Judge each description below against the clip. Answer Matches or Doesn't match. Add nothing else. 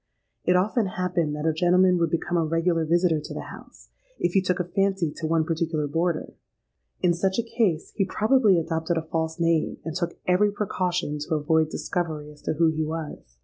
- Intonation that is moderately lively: Doesn't match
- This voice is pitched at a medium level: Matches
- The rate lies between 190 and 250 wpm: Matches